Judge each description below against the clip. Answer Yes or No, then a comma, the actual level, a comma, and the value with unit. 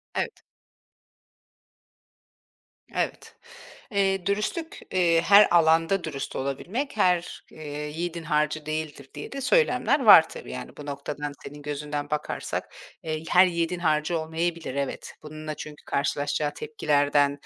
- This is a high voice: No, medium, 160 Hz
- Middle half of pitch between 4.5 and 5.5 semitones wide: No, average, 3.5 semitones